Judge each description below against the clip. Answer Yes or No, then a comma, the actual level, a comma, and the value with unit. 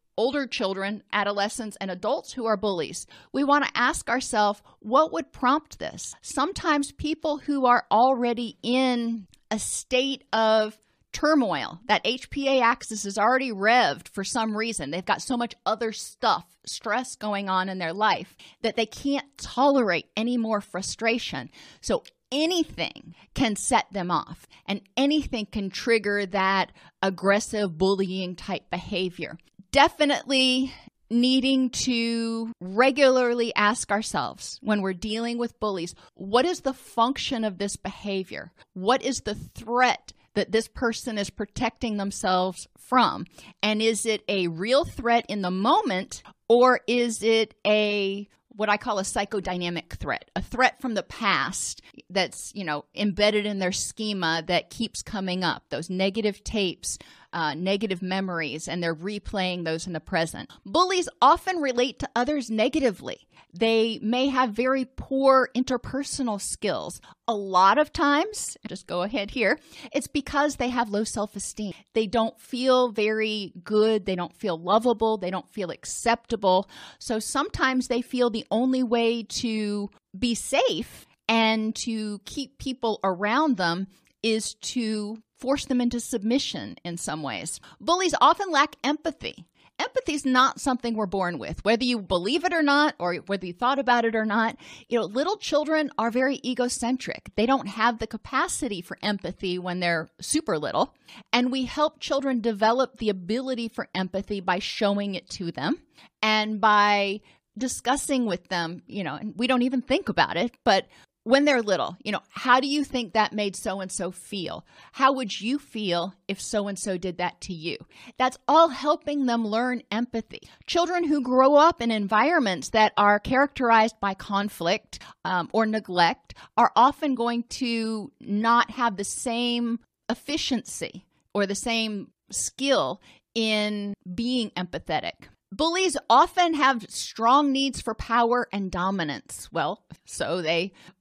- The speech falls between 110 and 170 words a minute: Yes, average, 155 wpm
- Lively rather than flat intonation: No, average, 4.4 semitones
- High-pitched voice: Yes, high, 225 Hz